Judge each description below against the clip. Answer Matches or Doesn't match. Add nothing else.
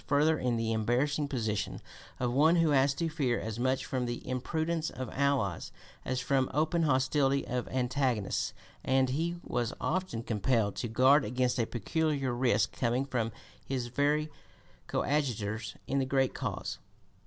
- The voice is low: Matches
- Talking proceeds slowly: Doesn't match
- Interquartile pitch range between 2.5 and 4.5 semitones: Matches